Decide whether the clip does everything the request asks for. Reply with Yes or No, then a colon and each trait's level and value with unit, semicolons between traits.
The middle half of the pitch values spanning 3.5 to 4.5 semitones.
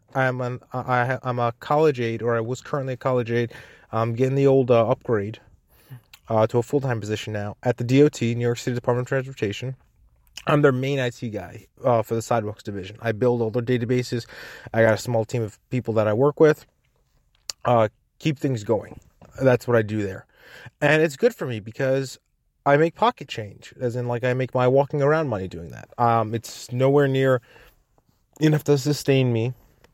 No: average, 2.9 semitones